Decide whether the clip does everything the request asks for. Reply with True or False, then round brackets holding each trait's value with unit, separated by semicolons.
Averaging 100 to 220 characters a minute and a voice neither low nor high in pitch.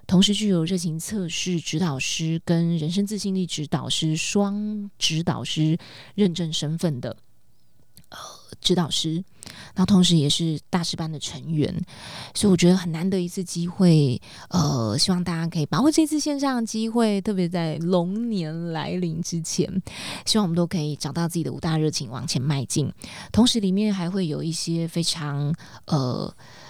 False (255 characters per minute; 170 Hz)